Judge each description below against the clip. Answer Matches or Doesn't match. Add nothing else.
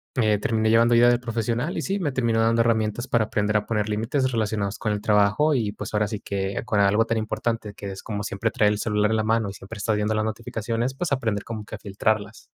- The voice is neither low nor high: Doesn't match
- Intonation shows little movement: Matches